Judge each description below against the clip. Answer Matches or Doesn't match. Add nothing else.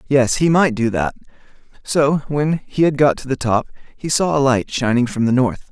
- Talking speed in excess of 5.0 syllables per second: Doesn't match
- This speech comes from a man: Matches